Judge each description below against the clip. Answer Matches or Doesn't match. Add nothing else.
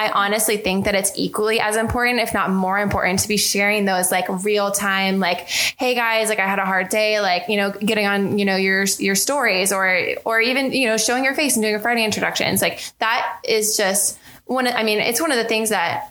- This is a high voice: Matches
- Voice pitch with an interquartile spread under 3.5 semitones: Matches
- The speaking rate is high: Matches